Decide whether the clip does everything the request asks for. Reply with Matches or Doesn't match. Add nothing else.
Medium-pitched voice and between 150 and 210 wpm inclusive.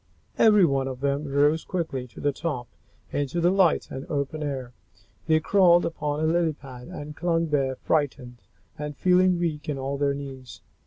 Matches